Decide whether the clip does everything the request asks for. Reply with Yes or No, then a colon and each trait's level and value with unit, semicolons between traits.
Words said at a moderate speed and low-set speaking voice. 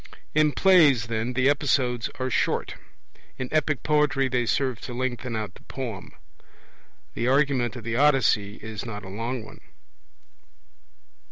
Yes: average, 145 wpm; low, 125 Hz